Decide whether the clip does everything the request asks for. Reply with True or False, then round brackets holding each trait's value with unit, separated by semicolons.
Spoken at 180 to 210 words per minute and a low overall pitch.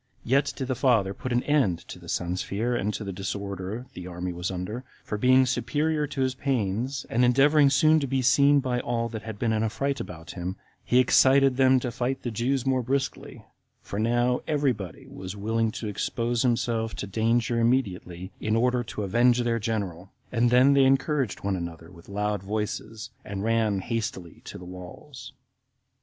True (195 wpm; 115 Hz)